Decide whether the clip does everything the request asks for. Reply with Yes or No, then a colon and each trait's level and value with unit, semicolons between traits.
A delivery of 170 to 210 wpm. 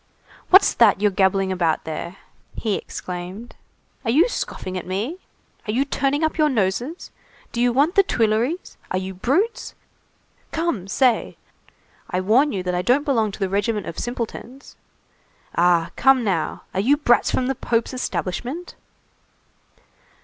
No: average, 155 wpm